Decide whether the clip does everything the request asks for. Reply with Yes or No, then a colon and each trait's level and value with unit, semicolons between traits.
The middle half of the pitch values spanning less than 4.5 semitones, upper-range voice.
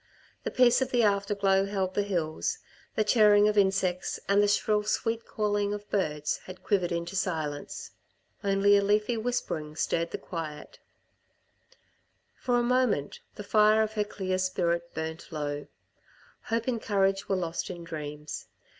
Yes: average, 3.7 semitones; high, 200 Hz